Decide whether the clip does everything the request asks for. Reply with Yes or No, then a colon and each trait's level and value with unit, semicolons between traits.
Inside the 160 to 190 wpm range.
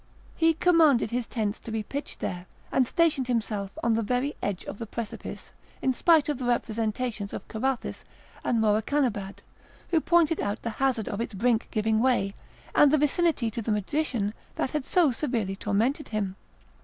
Yes: average, 175 wpm